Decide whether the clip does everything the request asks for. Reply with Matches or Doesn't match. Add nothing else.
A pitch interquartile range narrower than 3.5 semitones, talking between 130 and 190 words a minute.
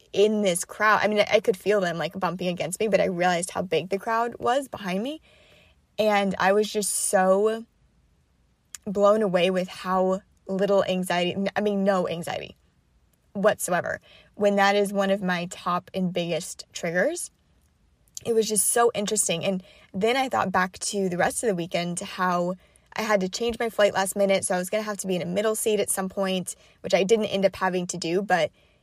Doesn't match